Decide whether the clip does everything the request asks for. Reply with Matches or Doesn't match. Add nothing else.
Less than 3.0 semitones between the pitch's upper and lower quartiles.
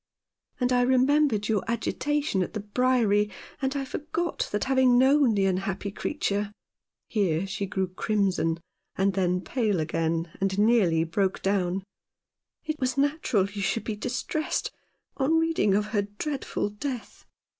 Doesn't match